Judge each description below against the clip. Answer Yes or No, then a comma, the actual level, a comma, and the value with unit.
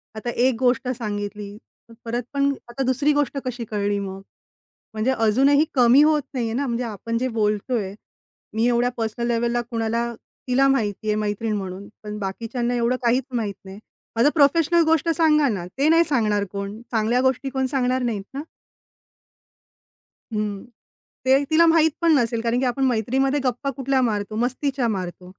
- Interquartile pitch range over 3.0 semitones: Yes, average, 4.0 semitones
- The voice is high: Yes, high, 240 Hz